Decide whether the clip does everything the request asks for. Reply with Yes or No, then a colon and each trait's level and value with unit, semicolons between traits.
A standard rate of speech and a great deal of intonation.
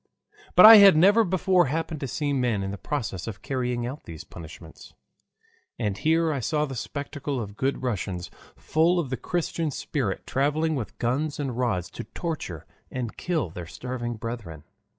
Yes: average, 170 wpm; wide, 6.3 semitones